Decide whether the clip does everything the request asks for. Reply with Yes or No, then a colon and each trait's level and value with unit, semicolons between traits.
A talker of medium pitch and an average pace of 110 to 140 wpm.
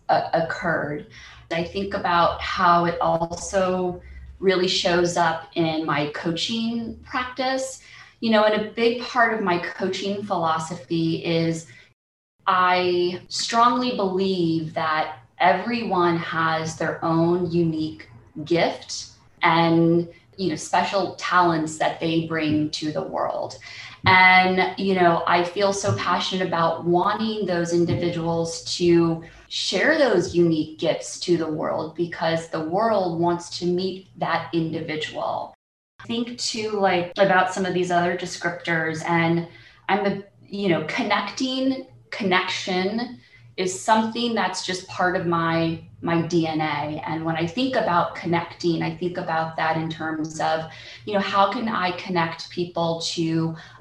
Yes: medium, 170 Hz; slow, 135 wpm